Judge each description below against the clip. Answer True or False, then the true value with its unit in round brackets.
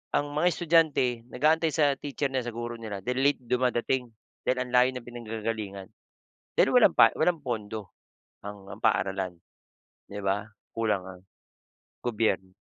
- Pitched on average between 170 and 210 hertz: False (120 Hz)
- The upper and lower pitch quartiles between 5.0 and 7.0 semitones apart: False (4.6 semitones)